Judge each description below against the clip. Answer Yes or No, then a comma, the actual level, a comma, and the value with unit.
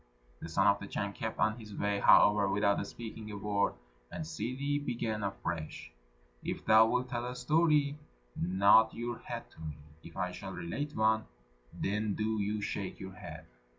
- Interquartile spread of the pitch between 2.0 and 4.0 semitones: Yes, average, 3.1 semitones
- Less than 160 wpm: No, average, 175 wpm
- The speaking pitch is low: Yes, low, 105 Hz